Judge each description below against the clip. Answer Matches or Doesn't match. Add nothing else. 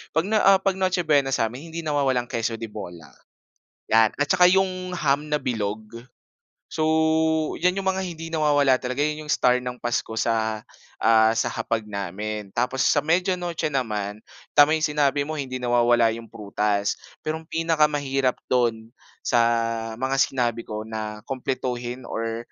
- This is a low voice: Matches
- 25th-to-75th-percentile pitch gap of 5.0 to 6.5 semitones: Matches